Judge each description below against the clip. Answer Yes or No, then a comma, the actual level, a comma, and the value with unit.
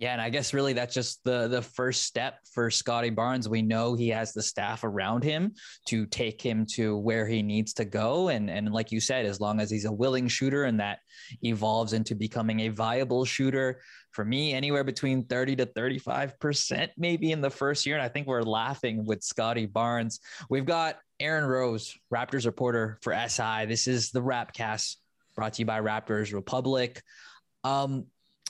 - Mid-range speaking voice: No, low, 120 Hz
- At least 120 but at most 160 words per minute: No, average, 190 wpm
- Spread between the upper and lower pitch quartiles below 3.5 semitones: Yes, average, 3.0 semitones